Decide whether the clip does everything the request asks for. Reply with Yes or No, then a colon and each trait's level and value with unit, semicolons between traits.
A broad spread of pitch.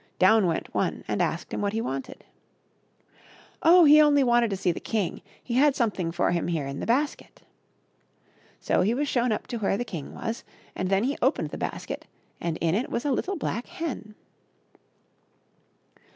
Yes: wide, 6.8 semitones